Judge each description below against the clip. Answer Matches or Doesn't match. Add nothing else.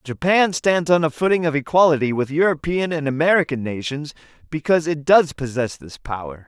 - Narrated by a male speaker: Matches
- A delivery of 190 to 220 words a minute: Doesn't match